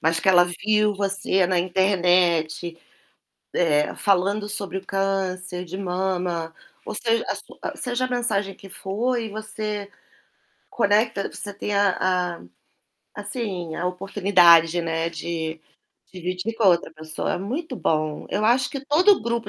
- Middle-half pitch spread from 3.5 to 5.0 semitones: No, average, 3.1 semitones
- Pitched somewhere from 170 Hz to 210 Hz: Yes, high, 190 Hz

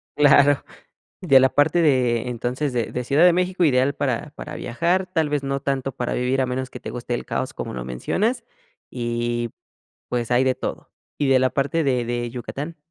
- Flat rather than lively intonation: No, average, 3.3 semitones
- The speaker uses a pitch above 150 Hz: No, low, 130 Hz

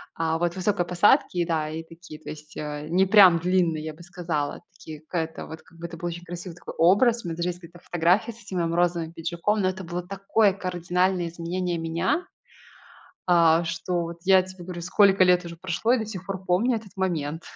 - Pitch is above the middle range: No, medium, 175 Hz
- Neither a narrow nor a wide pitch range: No, narrow, 2.1 semitones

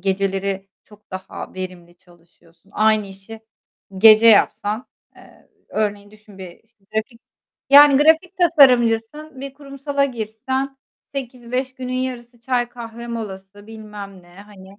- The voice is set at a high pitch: Yes, high, 220 Hz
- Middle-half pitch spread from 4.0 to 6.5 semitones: Yes, average, 4.6 semitones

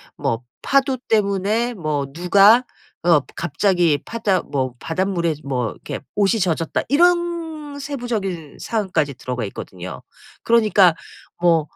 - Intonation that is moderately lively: No, wide, 6.5 semitones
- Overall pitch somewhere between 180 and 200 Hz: Yes, medium, 185 Hz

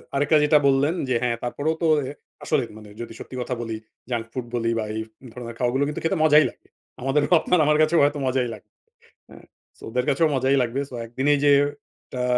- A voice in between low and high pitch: No, low, 130 Hz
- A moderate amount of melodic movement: Yes, average, 3.4 semitones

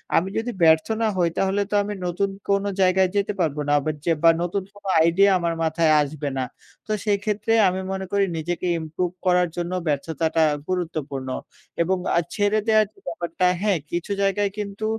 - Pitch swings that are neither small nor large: Yes, average, 3.5 semitones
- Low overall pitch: No, medium, 180 Hz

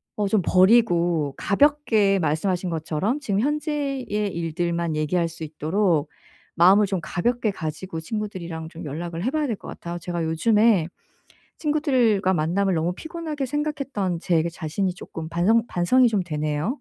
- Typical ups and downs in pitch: No, wide, 5.7 semitones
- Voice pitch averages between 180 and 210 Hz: Yes, medium, 185 Hz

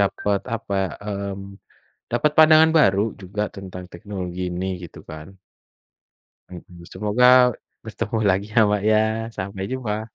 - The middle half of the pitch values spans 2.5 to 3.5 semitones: Yes, average, 2.9 semitones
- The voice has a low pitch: Yes, low, 100 Hz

